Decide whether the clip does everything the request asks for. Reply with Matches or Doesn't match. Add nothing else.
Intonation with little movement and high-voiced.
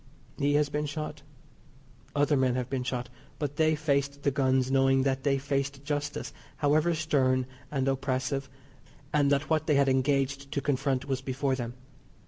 Doesn't match